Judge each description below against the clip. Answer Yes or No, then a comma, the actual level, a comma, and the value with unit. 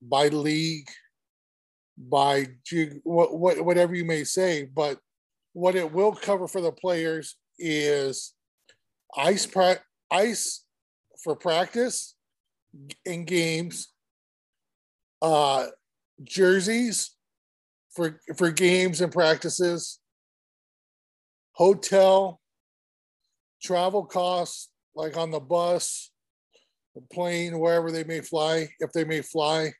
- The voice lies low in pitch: No, medium, 165 Hz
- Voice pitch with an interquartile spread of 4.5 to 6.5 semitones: No, average, 3.6 semitones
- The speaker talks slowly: Yes, slow, 95 wpm